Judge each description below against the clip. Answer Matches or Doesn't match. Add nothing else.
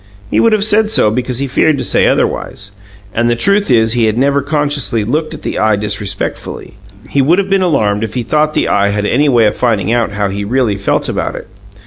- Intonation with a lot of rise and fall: Matches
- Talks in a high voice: Doesn't match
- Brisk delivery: Matches